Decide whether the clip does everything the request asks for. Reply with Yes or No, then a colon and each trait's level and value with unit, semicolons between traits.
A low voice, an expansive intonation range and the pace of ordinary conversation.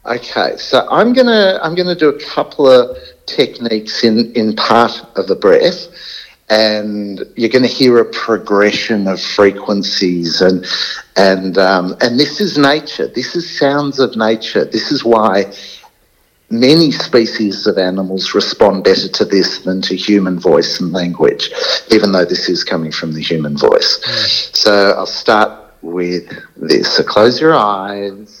Yes: low, 110 Hz; wide, 7.4 semitones; average, 160 wpm